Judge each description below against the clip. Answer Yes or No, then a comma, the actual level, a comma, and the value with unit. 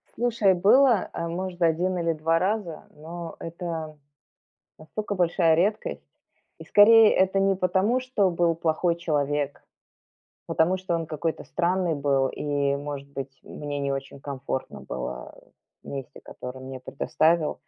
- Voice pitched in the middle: Yes, medium, 165 Hz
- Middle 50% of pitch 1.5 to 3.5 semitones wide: No, average, 4.6 semitones